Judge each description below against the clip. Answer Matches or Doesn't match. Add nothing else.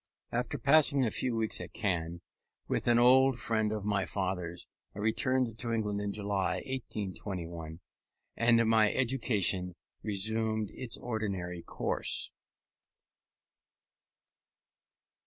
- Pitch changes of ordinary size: Matches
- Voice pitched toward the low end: Matches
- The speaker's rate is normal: Doesn't match